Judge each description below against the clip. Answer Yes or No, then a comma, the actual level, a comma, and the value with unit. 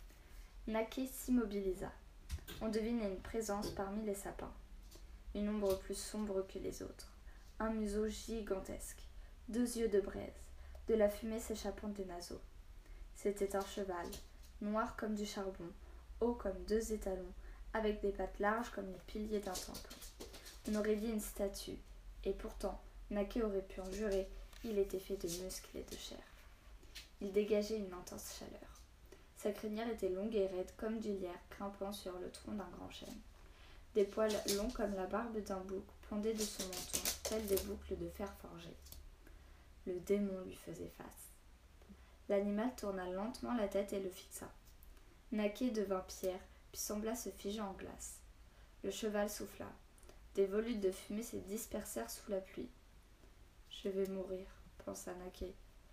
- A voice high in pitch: Yes, high, 200 Hz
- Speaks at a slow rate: No, average, 160 wpm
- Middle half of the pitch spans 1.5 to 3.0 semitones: Yes, narrow, 2.4 semitones